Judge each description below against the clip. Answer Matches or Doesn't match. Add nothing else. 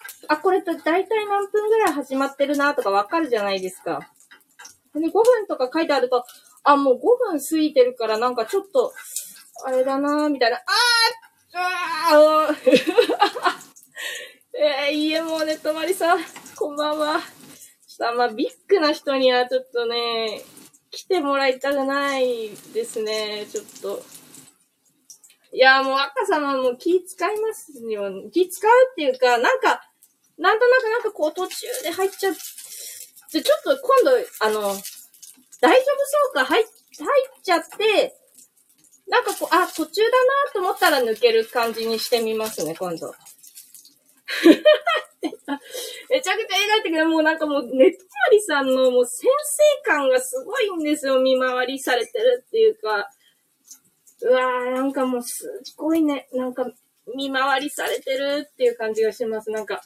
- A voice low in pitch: Doesn't match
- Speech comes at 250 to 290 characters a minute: Doesn't match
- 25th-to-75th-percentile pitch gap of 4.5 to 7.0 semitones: Doesn't match